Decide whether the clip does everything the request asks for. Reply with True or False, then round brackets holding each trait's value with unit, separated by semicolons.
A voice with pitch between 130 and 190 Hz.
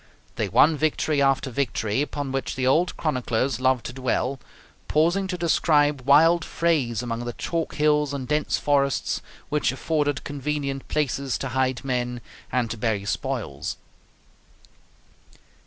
True (140 Hz)